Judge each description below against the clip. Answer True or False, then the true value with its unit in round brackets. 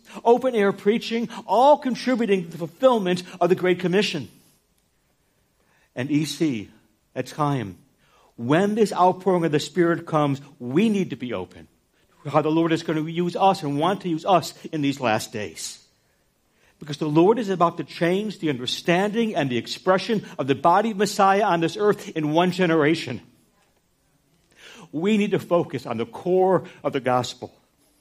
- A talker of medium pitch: True (170 Hz)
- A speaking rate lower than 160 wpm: False (170 wpm)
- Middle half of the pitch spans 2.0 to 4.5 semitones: False (5.3 semitones)